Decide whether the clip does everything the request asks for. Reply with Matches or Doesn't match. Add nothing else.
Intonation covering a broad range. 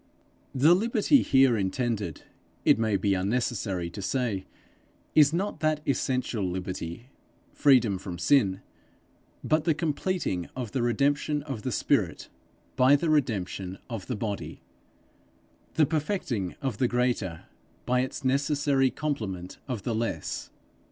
Matches